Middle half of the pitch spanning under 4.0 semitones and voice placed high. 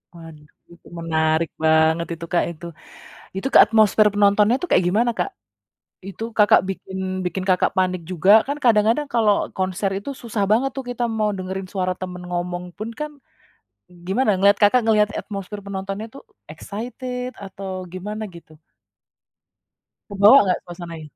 Yes: average, 3.3 semitones; high, 195 Hz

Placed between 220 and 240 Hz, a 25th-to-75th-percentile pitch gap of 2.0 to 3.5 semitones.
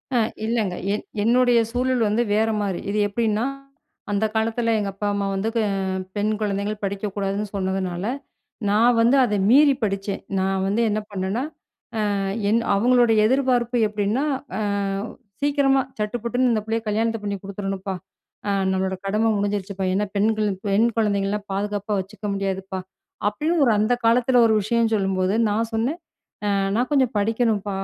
No: high, 210 Hz; average, 2.8 semitones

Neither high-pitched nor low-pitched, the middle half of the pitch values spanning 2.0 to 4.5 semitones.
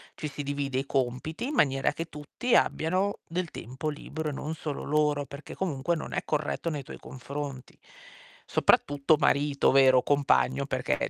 Yes: medium, 145 Hz; narrow, 2.4 semitones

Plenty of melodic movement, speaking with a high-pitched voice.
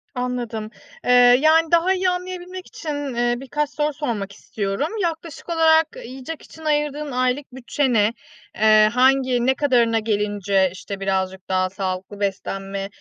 Yes: wide, 6.6 semitones; very high, 250 Hz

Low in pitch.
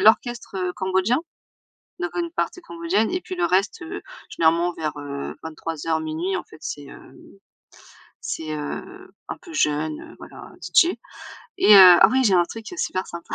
No: high, 190 Hz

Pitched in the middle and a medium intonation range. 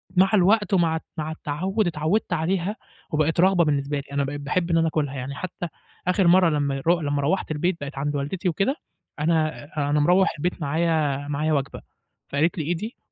Yes: medium, 160 Hz; average, 3.7 semitones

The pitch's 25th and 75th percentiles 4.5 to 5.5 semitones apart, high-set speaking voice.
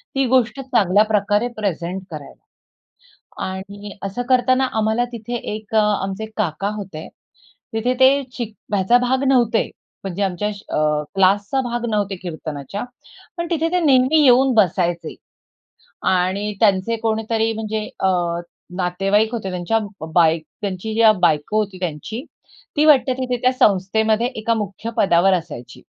No: average, 4.1 semitones; high, 210 Hz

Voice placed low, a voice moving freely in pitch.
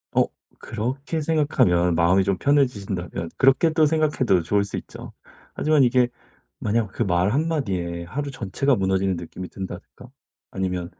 Yes: low, 100 Hz; wide, 7.4 semitones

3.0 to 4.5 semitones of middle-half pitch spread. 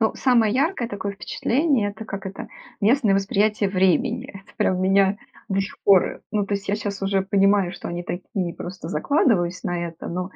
No: narrow, 2.4 semitones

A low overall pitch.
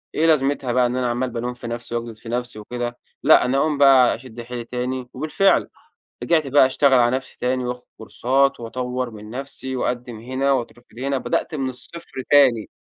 Yes: low, 125 Hz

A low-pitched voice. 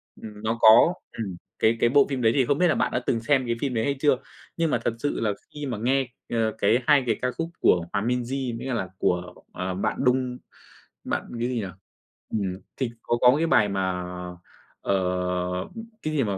Yes: low, 120 Hz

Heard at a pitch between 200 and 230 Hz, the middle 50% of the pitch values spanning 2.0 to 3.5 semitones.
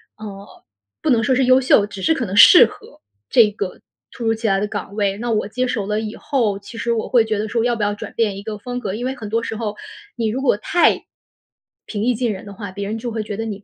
Yes: high, 220 Hz; average, 2.7 semitones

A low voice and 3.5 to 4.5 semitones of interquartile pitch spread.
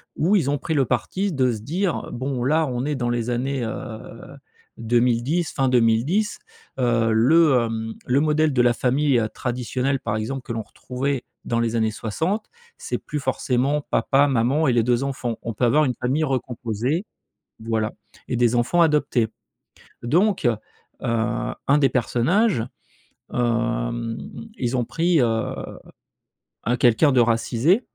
Yes: low, 125 Hz; average, 3.8 semitones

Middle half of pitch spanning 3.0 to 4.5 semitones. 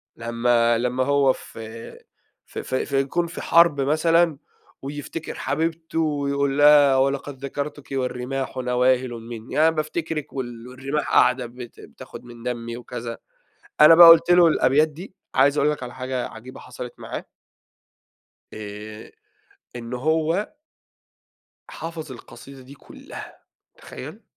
Yes: average, 3.7 semitones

